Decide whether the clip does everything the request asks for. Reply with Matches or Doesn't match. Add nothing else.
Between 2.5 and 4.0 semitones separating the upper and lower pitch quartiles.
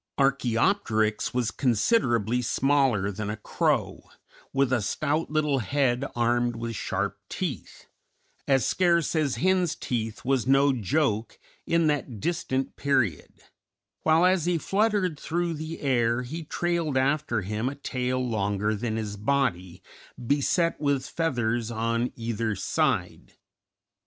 Doesn't match